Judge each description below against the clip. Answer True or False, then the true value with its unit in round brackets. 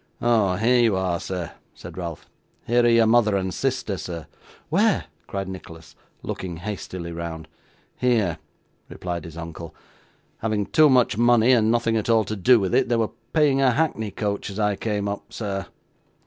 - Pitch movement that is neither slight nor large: True (4.6 semitones)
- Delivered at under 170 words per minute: False (175 wpm)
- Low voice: True (105 Hz)